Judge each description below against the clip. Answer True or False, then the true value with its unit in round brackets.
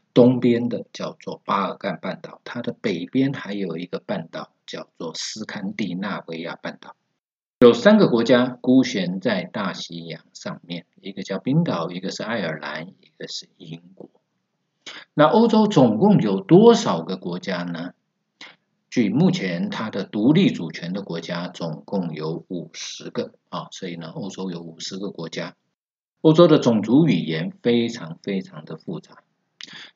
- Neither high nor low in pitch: False (120 Hz)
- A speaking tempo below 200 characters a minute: False (230 characters per minute)